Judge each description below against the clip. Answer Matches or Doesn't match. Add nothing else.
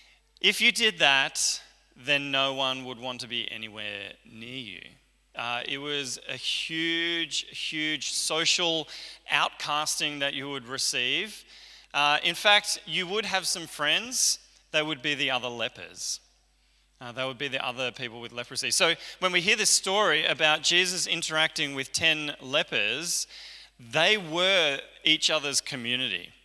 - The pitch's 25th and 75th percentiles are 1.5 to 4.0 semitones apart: Doesn't match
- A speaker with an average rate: Matches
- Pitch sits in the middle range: Matches